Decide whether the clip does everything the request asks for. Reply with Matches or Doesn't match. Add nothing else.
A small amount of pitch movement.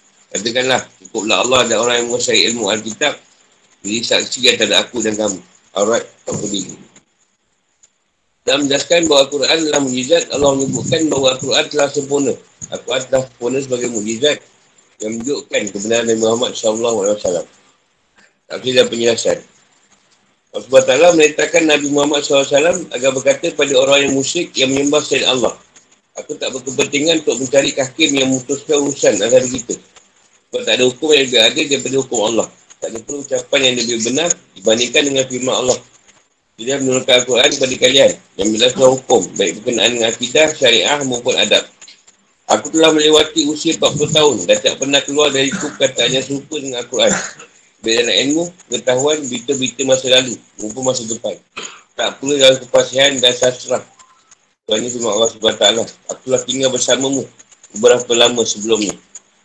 Doesn't match